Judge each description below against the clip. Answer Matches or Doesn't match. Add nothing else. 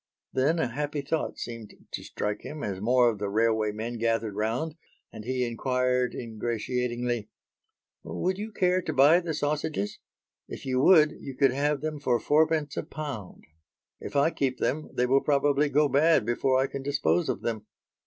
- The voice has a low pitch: Matches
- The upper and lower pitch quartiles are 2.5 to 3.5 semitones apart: Doesn't match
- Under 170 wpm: Doesn't match